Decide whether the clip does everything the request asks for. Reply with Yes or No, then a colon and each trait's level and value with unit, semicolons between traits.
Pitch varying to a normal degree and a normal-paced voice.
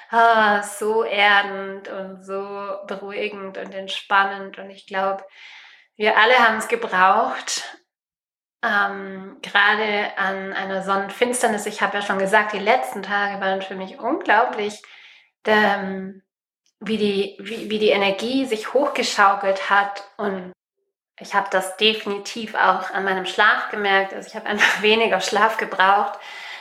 No: narrow, 1.9 semitones; average, 135 wpm